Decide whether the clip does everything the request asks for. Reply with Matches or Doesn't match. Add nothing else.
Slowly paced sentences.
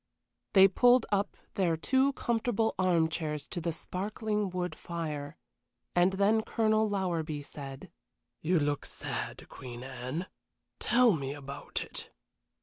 Matches